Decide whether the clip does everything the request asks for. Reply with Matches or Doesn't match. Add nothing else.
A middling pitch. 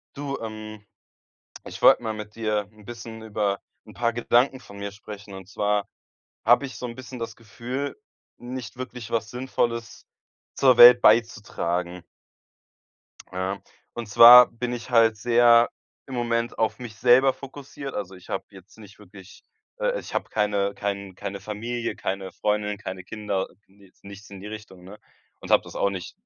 Doesn't match